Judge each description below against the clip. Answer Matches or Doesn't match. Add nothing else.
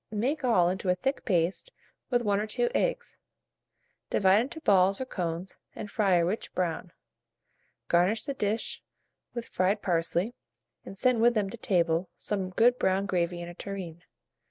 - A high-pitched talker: Matches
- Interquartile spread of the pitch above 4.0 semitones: Matches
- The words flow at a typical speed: Matches